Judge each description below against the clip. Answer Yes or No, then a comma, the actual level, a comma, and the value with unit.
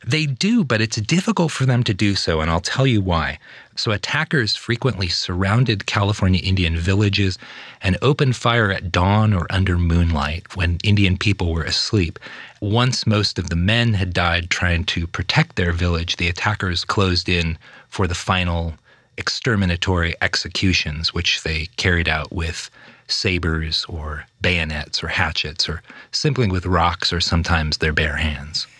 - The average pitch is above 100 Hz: No, very low, 90 Hz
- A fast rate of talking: No, average, 155 wpm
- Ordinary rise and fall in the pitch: Yes, average, 4.0 semitones